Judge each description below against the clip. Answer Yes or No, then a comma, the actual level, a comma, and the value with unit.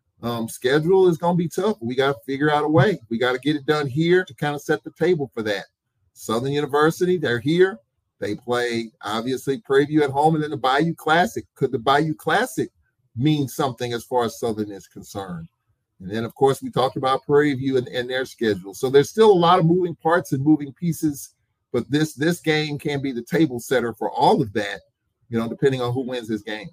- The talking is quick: Yes, fast, 230 wpm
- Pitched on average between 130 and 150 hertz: Yes, low, 135 Hz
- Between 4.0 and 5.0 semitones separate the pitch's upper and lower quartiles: Yes, average, 4.7 semitones